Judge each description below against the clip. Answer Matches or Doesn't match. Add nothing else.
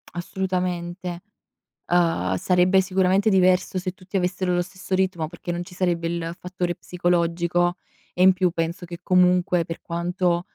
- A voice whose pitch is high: Doesn't match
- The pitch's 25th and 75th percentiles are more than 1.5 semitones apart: Doesn't match